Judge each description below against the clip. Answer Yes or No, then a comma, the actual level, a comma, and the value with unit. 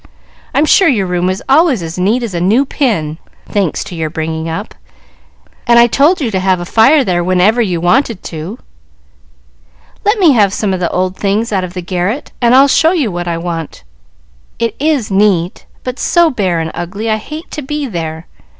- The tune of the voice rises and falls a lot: Yes, wide, 6.5 semitones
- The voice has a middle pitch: No, high, 200 Hz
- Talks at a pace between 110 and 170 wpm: No, average, 195 wpm